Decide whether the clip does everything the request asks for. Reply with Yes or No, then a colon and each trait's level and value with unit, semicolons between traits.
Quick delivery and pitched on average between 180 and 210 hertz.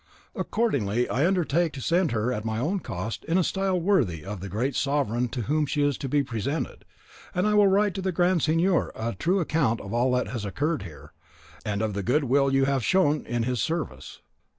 No: fast, 220 wpm; medium, 140 Hz